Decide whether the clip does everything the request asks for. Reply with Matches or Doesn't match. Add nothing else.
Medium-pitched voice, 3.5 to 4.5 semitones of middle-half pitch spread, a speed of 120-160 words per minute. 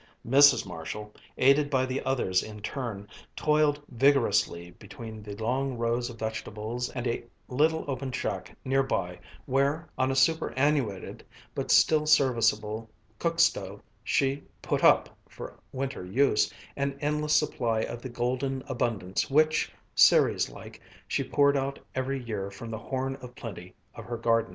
Doesn't match